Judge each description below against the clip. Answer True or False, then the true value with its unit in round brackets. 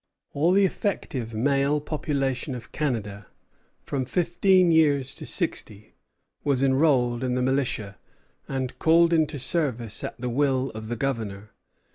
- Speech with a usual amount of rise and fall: True (4.1 semitones)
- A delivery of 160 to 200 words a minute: False (135 wpm)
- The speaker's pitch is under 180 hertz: True (135 Hz)